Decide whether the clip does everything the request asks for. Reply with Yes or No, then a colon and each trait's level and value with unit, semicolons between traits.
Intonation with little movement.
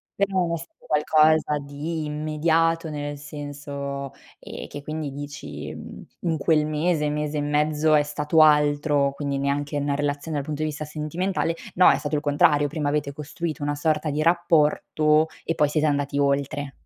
Yes: narrow, 1.3 semitones